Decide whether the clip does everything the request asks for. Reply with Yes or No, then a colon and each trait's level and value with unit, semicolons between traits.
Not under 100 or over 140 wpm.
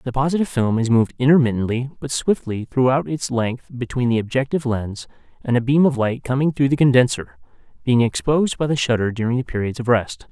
No: average, 200 wpm